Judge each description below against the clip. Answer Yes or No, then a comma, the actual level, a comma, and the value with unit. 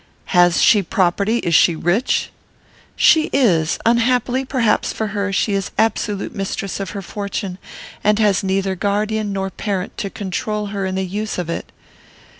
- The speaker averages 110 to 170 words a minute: Yes, average, 160 wpm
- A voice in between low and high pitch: No, high, 200 Hz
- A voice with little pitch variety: Yes, narrow, 2.2 semitones